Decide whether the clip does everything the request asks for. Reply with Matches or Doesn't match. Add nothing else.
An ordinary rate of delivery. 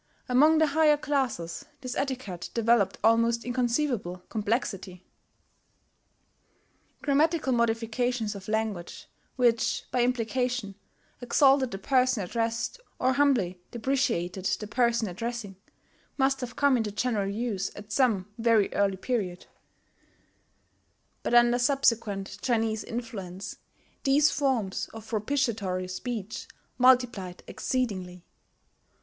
Doesn't match